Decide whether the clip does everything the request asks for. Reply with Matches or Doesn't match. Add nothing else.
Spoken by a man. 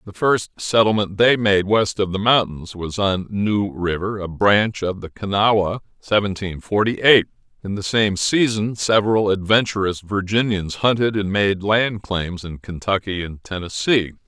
Matches